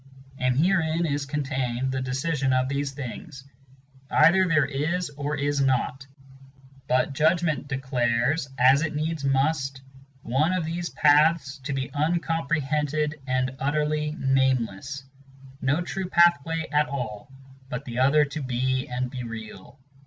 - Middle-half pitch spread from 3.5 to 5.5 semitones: No, average, 2.8 semitones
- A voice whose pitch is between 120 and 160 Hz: Yes, medium, 140 Hz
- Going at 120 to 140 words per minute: Yes, slow, 135 wpm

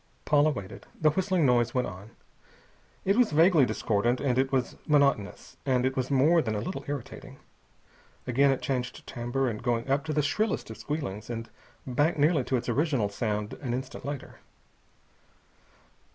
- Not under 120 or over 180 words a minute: Yes, average, 165 wpm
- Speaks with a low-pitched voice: Yes, low, 130 Hz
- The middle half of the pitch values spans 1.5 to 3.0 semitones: No, average, 3.7 semitones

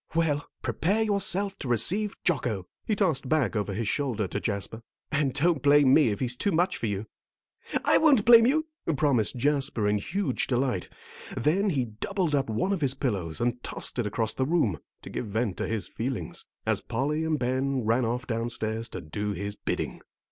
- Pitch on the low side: Yes, low, 130 Hz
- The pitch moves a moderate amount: No, wide, 6.2 semitones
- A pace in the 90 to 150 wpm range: No, average, 190 wpm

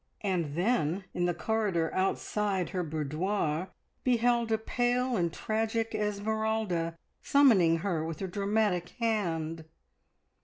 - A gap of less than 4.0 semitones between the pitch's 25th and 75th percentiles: No, average, 4.8 semitones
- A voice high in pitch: Yes, high, 195 Hz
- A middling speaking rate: No, slow, 115 wpm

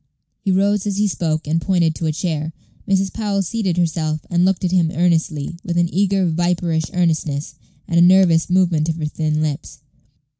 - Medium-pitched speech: Yes, medium, 170 Hz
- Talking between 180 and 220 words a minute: Yes, average, 185 wpm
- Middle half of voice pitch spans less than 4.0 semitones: Yes, average, 2.9 semitones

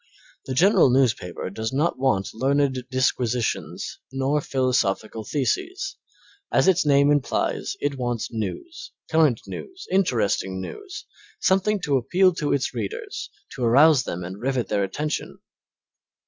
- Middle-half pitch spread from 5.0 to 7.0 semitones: Yes, wide, 5.6 semitones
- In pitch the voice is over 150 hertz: No, low, 130 Hz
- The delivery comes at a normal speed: No, slow, 130 wpm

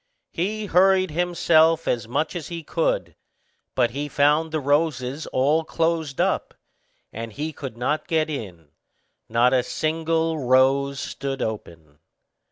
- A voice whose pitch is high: No, medium, 150 Hz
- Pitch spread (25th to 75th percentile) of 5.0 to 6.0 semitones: No, average, 4.2 semitones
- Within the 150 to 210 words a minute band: No, slow, 135 wpm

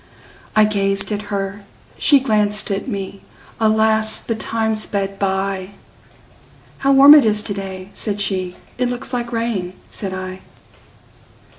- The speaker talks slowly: Yes, slow, 125 wpm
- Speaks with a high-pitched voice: Yes, high, 210 Hz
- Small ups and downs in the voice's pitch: Yes, narrow, 2.2 semitones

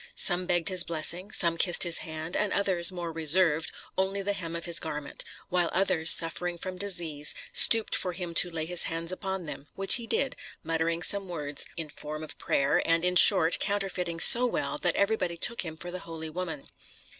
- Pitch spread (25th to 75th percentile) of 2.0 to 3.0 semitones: Yes, narrow, 2.5 semitones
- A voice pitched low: No, medium, 175 Hz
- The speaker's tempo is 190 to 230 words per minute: Yes, average, 195 wpm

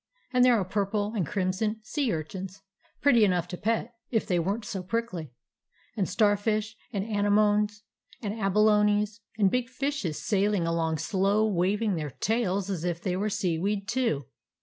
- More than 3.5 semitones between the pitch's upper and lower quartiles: No, average, 2.8 semitones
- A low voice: No, high, 205 Hz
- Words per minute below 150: No, average, 165 wpm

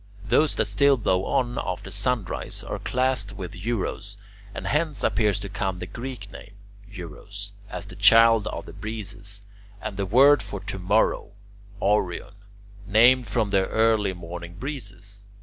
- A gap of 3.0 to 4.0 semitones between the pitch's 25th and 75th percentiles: Yes, average, 3.3 semitones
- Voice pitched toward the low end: Yes, low, 105 Hz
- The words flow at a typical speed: Yes, average, 160 wpm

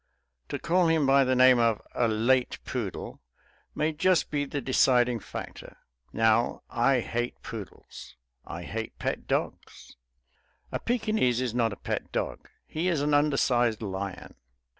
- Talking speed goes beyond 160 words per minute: No, average, 145 wpm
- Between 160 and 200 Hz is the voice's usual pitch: No, low, 125 Hz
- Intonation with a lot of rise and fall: No, average, 4.3 semitones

